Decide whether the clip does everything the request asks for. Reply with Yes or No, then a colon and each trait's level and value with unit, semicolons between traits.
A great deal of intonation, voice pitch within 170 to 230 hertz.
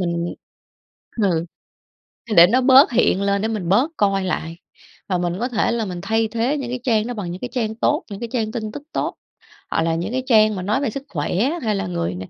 No: average, 4.8 semitones; high, 215 Hz